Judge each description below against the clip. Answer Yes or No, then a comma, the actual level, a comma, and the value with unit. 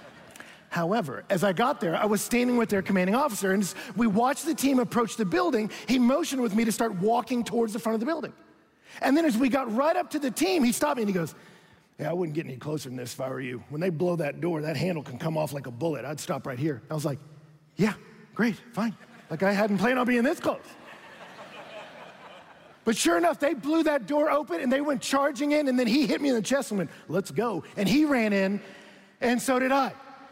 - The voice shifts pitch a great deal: Yes, wide, 7.1 semitones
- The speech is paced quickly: Yes, fast, 250 wpm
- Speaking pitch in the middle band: No, high, 225 Hz